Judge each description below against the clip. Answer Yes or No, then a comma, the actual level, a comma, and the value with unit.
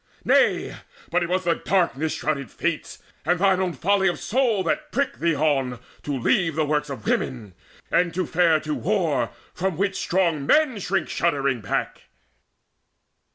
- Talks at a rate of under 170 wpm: Yes, average, 160 wpm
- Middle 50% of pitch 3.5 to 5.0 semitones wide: Yes, average, 4.5 semitones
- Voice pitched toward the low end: No, medium, 170 Hz